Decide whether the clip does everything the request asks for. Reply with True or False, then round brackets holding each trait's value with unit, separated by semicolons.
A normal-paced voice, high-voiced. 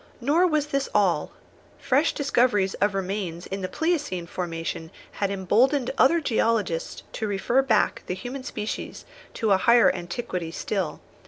True (145 wpm; 210 Hz)